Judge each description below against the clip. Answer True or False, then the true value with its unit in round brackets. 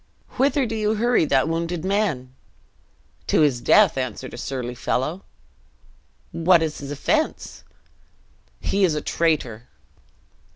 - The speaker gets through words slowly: True (125 wpm)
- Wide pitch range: True (7.3 semitones)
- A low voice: False (165 Hz)